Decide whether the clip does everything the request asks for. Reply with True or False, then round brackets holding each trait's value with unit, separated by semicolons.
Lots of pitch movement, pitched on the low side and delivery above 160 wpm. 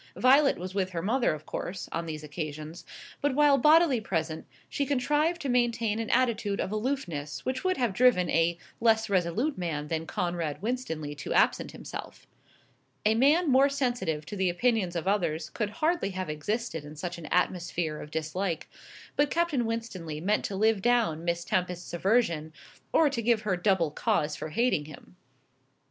False (6.9 semitones; 195 Hz; 170 wpm)